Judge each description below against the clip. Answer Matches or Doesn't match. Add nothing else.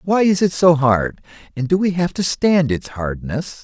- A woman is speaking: Doesn't match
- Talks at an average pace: Doesn't match